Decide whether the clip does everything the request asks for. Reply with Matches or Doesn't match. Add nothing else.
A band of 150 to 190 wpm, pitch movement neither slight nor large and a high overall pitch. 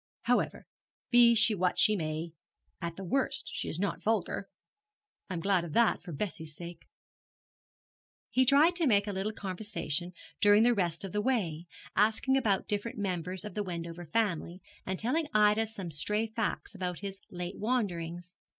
Matches